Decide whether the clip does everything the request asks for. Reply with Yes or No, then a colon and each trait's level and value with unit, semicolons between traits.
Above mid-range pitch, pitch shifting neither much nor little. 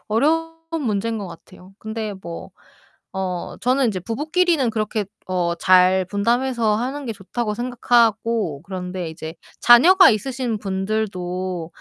Yes: high, 215 Hz; average, 4.5 semitones